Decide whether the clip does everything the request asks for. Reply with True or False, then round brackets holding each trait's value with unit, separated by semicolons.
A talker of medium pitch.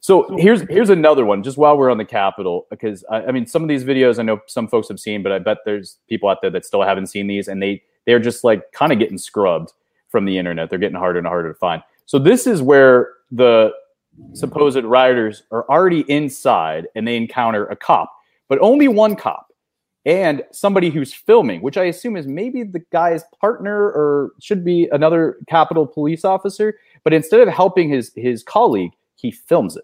True (145 Hz)